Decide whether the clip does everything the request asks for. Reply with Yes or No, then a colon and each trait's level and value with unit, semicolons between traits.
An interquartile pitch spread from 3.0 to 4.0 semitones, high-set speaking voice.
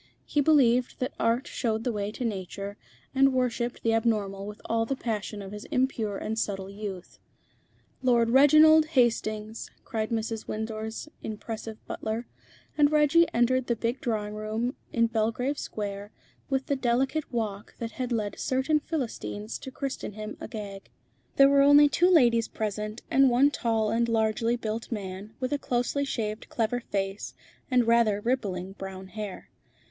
Yes: average, 3.4 semitones; high, 230 Hz